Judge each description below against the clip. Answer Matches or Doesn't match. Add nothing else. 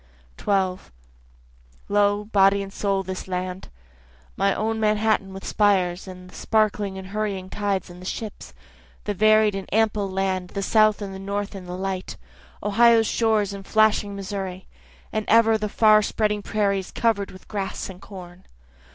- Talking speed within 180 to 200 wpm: Doesn't match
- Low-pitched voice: Doesn't match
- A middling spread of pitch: Doesn't match